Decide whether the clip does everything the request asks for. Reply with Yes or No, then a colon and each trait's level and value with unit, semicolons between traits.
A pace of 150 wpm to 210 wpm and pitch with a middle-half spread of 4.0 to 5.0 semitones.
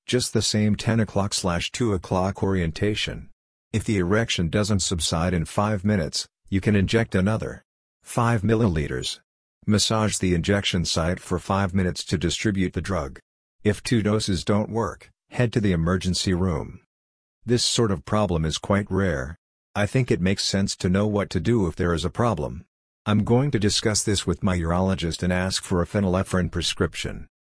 No: average, 175 wpm; average, 3.1 semitones